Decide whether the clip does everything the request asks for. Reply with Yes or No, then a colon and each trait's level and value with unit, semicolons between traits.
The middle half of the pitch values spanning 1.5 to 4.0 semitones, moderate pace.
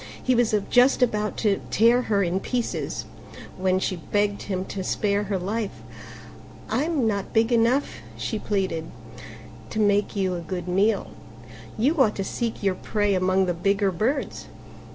Yes: average, 3.3 semitones; average, 155 wpm